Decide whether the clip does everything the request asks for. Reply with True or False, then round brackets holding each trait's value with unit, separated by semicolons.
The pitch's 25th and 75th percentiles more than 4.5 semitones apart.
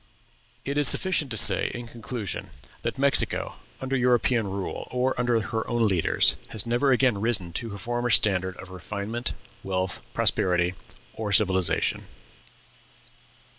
False (4.2 semitones)